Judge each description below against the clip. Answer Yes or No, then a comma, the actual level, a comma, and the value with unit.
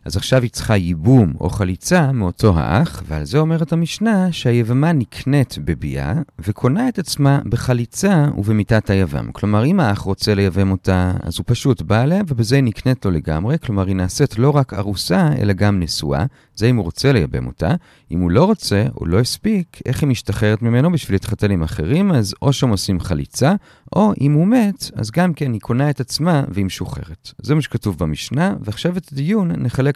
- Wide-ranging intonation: Yes, wide, 7.0 semitones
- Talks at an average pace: No, fast, 190 wpm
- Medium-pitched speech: No, low, 120 Hz